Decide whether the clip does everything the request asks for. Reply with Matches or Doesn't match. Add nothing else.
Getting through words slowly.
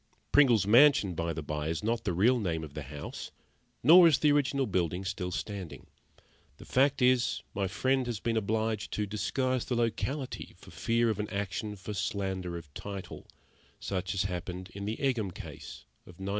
Doesn't match